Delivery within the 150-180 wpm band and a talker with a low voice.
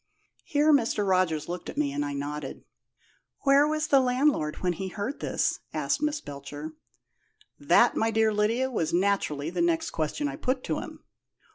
No: average, 170 wpm; high, 200 Hz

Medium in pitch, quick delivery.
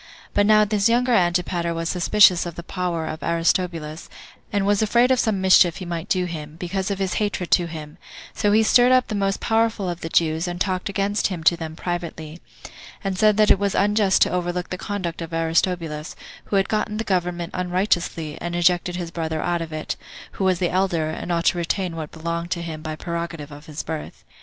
Yes: medium, 175 Hz; fast, 215 wpm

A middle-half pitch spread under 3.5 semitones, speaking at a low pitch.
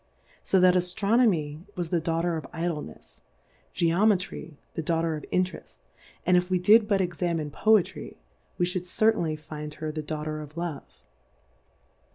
No: average, 2.9 semitones; medium, 170 Hz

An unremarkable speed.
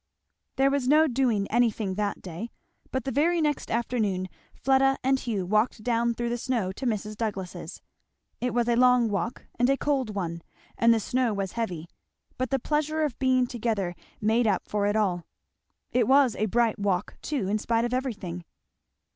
Yes: average, 180 wpm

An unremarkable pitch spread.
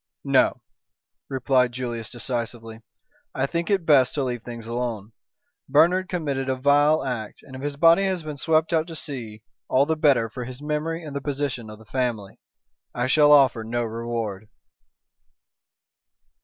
Yes: average, 4.2 semitones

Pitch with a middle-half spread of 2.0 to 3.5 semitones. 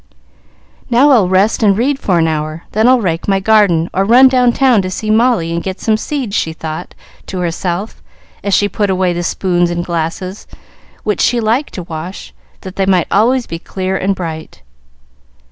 No: average, 4.3 semitones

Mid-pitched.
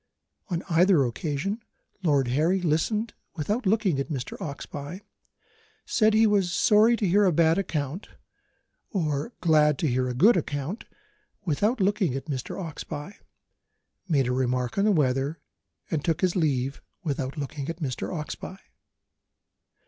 Yes: medium, 160 Hz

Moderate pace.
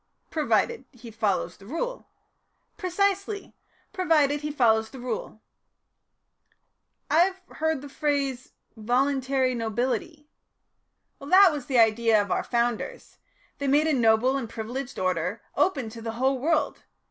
No: slow, 130 wpm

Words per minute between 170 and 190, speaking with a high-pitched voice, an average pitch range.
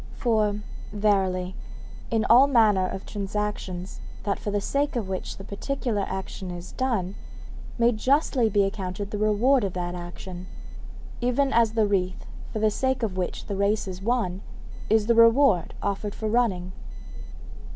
No: average, 155 wpm; high, 210 Hz; average, 3.5 semitones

